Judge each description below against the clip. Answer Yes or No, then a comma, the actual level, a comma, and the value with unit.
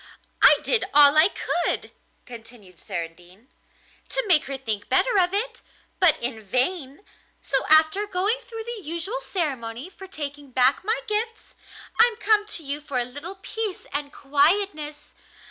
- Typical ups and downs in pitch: No, wide, 7.7 semitones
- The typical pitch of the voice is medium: No, very high, 310 Hz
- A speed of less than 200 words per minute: Yes, average, 150 wpm